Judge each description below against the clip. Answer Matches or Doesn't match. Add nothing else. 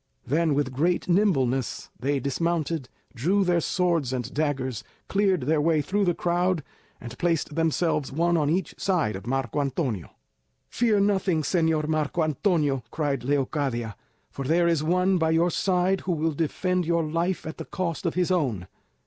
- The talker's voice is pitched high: Doesn't match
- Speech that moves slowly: Doesn't match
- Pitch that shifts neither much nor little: Matches